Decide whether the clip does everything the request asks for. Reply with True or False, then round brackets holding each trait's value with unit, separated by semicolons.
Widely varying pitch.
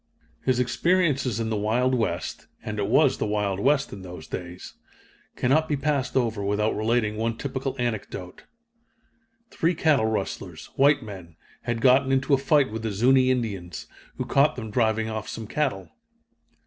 False (4.4 semitones)